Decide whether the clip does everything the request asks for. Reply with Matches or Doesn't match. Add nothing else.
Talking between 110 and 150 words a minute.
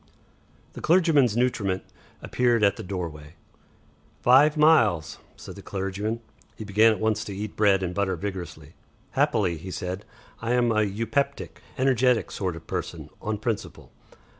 Matches